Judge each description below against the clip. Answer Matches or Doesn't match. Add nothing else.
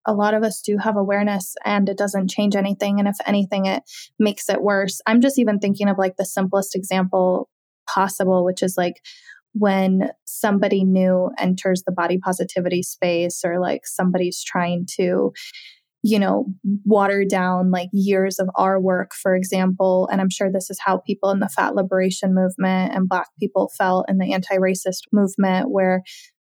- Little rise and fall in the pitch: Matches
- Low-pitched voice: Doesn't match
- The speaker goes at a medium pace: Matches